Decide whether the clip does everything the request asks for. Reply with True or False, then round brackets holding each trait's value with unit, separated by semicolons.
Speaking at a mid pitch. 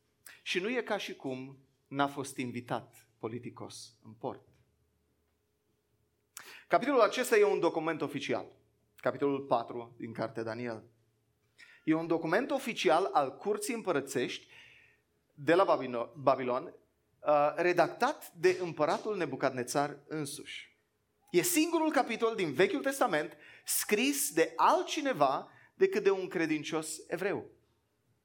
True (155 Hz)